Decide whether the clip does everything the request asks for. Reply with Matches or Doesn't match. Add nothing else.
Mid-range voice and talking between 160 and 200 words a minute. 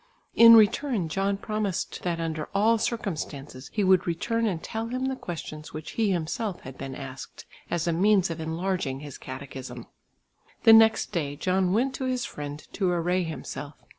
Matches